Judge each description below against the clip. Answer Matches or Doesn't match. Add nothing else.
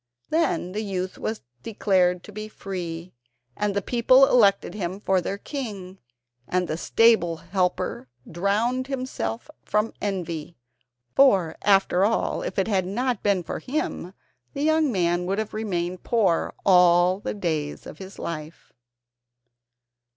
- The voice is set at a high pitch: Matches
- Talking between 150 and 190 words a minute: Doesn't match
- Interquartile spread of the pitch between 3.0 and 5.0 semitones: Matches